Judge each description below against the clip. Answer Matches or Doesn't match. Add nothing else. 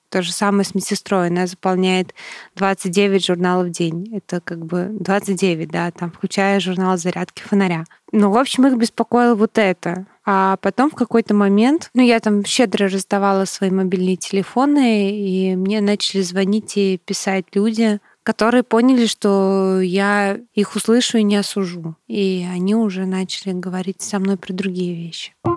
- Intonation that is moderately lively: Doesn't match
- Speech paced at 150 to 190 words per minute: Matches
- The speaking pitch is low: Doesn't match